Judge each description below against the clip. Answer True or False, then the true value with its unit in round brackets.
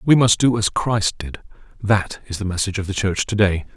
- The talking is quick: True (225 wpm)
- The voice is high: False (100 Hz)